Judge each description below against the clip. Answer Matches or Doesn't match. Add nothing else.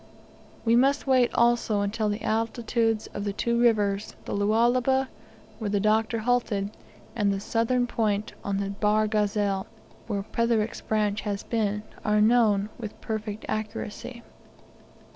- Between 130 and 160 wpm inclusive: Matches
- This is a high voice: Matches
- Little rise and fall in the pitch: Matches